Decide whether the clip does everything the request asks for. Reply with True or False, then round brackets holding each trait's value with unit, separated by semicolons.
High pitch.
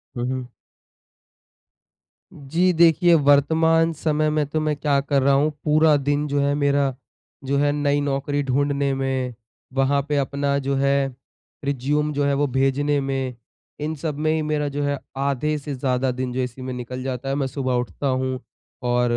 False (140 Hz)